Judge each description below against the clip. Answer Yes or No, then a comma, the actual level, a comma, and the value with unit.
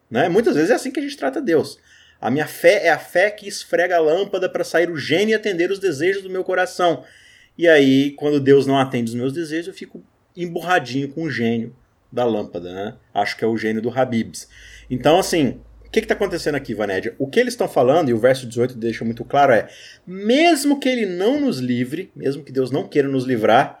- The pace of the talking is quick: Yes, fast, 230 wpm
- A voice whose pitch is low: No, medium, 150 Hz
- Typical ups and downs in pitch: No, wide, 7.6 semitones